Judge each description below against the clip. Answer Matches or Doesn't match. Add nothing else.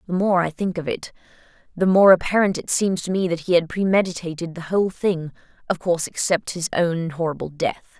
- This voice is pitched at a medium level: Matches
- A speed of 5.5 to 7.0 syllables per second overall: Matches